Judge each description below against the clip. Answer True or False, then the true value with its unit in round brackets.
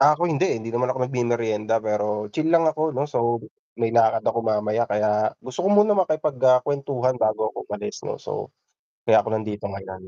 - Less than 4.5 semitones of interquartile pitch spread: False (5.1 semitones)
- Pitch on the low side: True (120 Hz)